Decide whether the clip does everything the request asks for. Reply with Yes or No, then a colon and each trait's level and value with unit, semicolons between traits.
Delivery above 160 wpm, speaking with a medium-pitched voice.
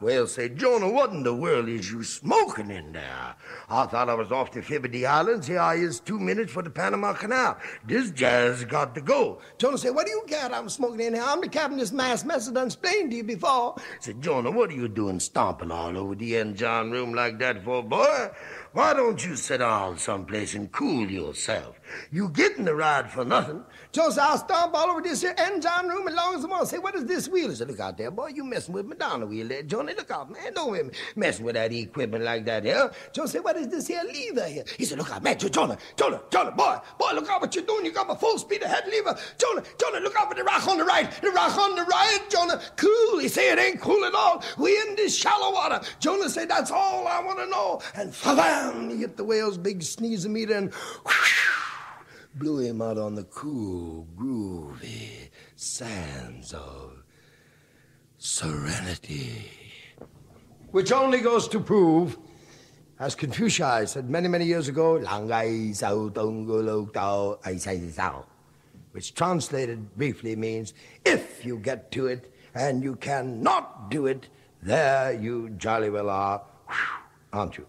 Yes: average, 200 wpm; medium, 155 Hz